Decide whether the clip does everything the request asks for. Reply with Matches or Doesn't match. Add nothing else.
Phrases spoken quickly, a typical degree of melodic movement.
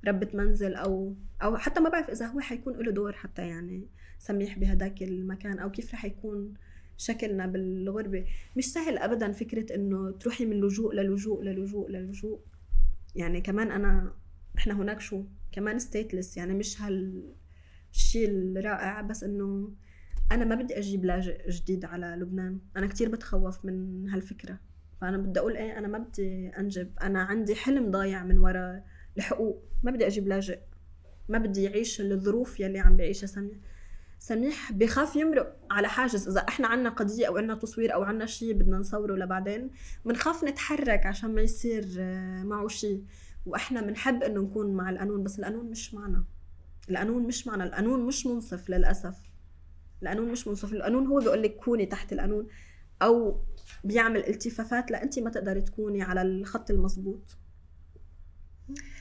Matches